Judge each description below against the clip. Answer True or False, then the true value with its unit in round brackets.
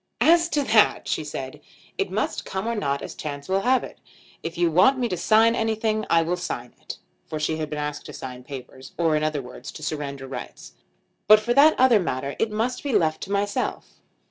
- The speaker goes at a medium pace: False (220 wpm)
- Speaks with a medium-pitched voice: True (170 Hz)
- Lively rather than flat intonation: True (7.0 semitones)